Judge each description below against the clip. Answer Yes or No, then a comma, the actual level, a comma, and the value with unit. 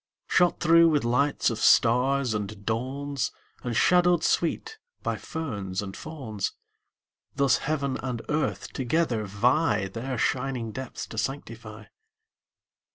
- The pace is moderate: No, slow, 120 wpm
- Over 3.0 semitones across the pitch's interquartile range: Yes, average, 4.8 semitones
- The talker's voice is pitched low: Yes, low, 130 Hz